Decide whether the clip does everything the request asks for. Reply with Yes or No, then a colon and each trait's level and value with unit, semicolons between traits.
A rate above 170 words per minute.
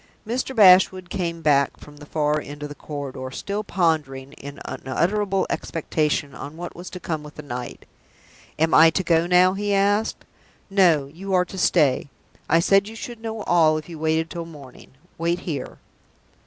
Yes: average, 180 wpm